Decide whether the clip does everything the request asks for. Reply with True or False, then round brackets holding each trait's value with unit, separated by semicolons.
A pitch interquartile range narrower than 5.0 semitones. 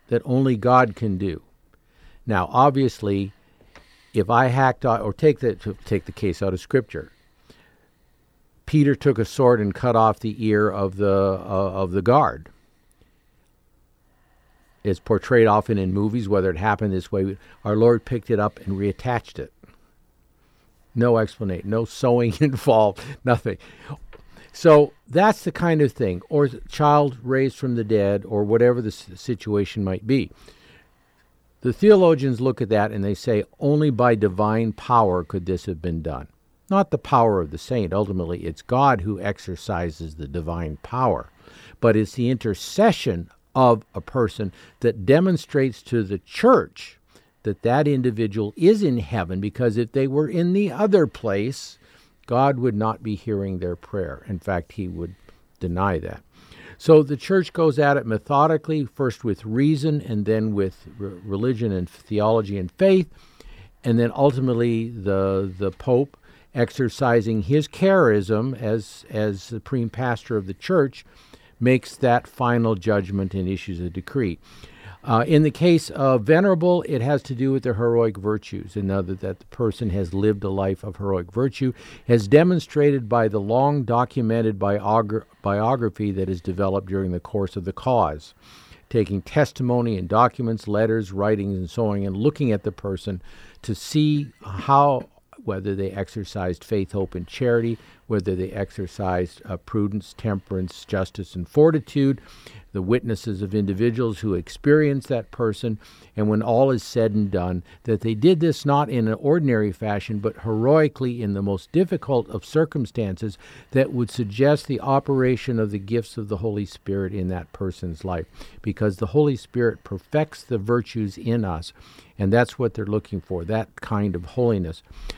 True (4.6 semitones)